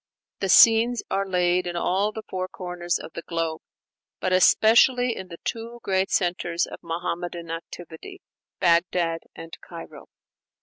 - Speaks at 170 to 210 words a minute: No, average, 140 wpm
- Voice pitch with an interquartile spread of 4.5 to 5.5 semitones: No, average, 2.9 semitones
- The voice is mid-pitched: Yes, medium, 180 Hz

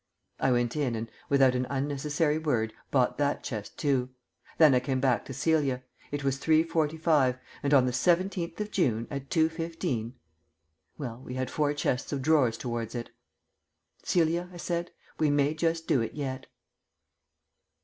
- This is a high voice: No, medium, 140 Hz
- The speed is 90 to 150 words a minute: No, average, 160 wpm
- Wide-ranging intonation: No, average, 4.0 semitones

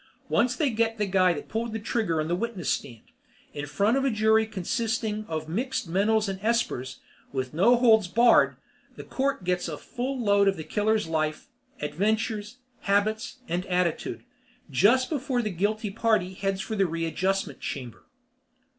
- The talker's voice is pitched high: Yes, high, 210 Hz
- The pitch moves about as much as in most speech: Yes, average, 4.3 semitones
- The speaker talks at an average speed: Yes, average, 170 wpm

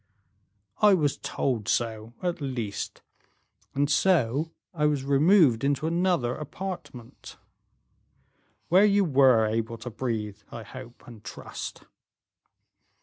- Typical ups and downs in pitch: No, wide, 6.2 semitones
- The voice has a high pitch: No, low, 135 Hz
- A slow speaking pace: Yes, slow, 110 wpm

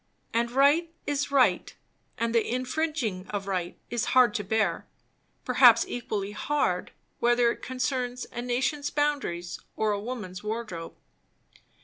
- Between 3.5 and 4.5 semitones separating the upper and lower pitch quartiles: Yes, average, 3.8 semitones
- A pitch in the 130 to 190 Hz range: No, high, 240 Hz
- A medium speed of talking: No, slow, 130 wpm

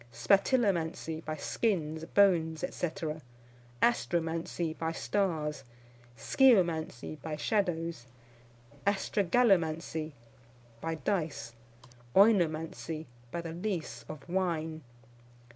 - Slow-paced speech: Yes, slow, 75 wpm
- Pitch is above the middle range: No, medium, 165 Hz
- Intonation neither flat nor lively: Yes, average, 3.5 semitones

